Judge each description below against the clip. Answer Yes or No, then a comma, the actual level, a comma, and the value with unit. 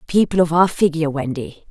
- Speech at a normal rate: Yes, average, 175 wpm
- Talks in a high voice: No, medium, 165 Hz